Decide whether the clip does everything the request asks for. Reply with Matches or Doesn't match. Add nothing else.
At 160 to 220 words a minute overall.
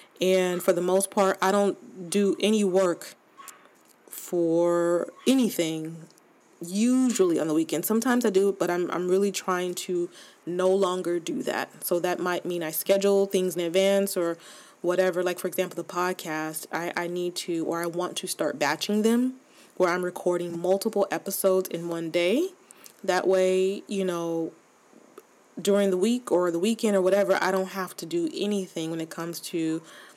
Matches